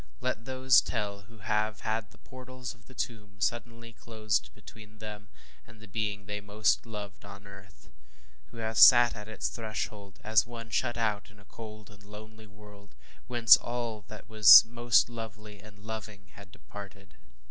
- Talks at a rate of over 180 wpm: No, average, 170 wpm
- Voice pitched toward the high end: No, low, 110 Hz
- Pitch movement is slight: Yes, narrow, 1.9 semitones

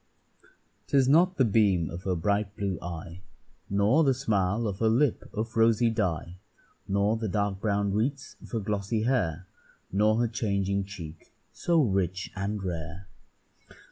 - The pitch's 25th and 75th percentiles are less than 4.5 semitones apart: Yes, average, 3.2 semitones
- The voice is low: Yes, low, 100 Hz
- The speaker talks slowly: No, average, 150 wpm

